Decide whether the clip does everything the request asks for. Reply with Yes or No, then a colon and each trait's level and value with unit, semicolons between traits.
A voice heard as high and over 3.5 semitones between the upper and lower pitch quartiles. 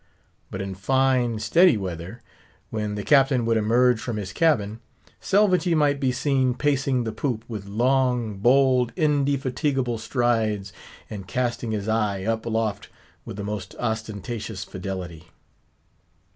No: low, 115 Hz; average, 4.2 semitones